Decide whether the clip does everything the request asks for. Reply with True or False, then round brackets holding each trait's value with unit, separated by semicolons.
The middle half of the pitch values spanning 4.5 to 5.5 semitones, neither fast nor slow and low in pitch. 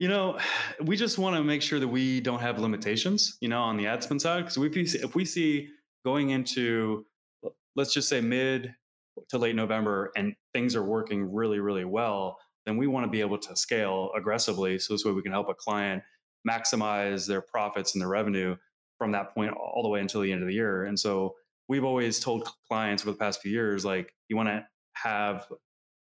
False (5.0 semitones; 215 wpm; 110 Hz)